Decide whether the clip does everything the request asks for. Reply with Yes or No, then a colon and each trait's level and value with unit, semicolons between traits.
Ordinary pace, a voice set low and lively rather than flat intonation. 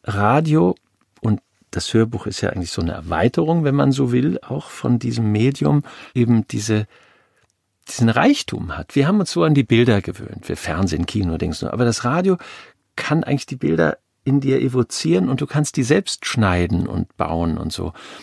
Yes: average, 180 wpm; low, 115 Hz; wide, 6.4 semitones